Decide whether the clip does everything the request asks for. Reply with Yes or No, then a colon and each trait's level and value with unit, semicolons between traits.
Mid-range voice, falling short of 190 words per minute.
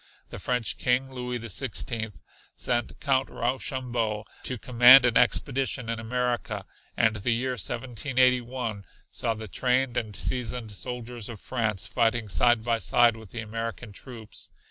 No: low, 120 Hz; average, 145 wpm